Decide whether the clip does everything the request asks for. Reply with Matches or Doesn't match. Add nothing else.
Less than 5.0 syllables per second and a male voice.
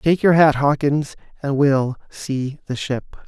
Matches